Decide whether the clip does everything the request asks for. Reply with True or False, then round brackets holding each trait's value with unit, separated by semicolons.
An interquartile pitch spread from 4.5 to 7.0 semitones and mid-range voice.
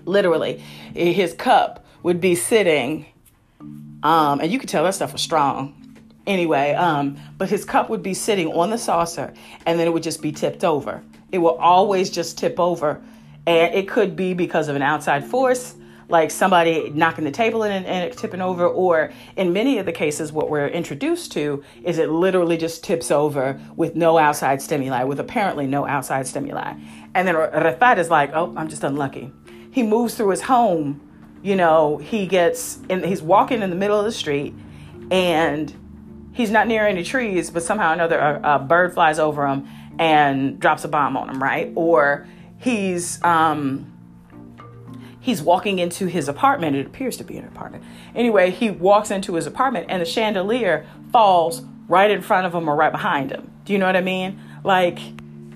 True (4.9 semitones; 170 Hz)